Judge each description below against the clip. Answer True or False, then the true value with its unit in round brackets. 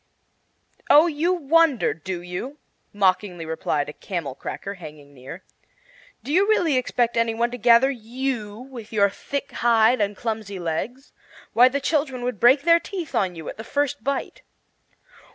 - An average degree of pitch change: False (6.1 semitones)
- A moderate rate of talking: True (160 wpm)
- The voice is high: True (235 Hz)